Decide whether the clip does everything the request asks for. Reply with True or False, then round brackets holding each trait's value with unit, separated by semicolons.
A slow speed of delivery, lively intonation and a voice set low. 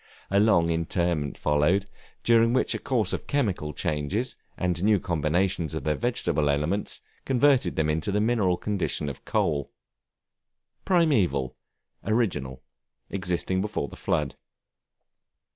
True (125 wpm; 6.0 semitones; 90 Hz)